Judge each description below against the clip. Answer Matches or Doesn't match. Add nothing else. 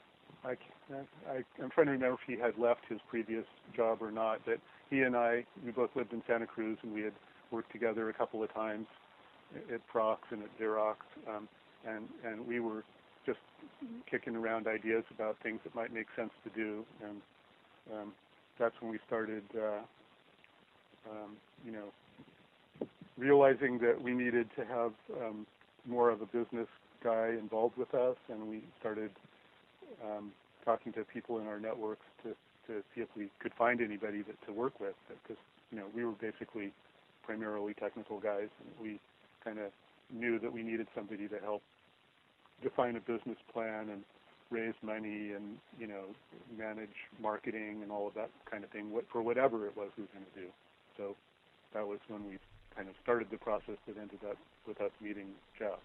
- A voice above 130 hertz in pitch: Doesn't match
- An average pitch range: Doesn't match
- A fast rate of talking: Doesn't match